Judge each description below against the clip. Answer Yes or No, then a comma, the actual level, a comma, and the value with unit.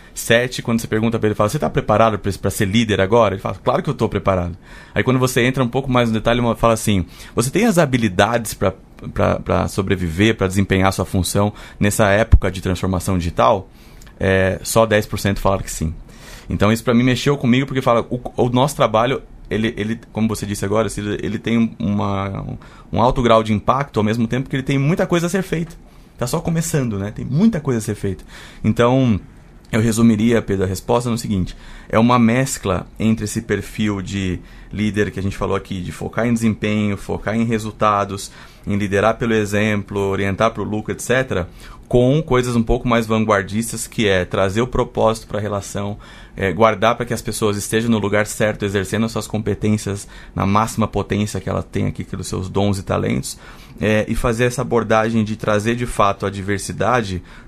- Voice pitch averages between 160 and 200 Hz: No, low, 110 Hz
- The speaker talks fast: Yes, fast, 195 wpm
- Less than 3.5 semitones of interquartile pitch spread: Yes, average, 2.9 semitones